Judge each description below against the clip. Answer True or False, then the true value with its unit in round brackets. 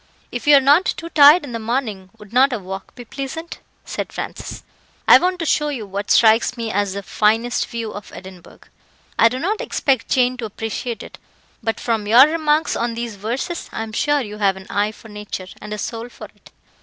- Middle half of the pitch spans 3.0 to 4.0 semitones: False (4.7 semitones)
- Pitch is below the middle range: False (230 Hz)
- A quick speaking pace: True (215 wpm)